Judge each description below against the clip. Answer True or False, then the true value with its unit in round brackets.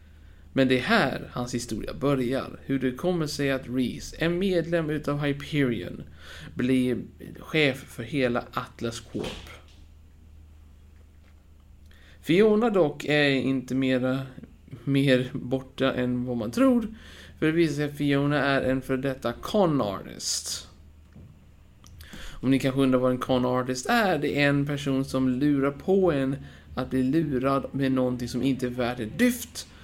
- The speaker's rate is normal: True (145 wpm)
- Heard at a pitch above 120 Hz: True (130 Hz)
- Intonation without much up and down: False (3.5 semitones)